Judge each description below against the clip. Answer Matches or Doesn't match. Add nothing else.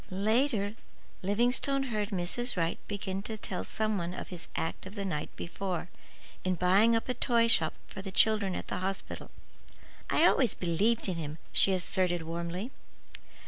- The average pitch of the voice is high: Matches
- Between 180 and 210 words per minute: Doesn't match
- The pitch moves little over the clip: Doesn't match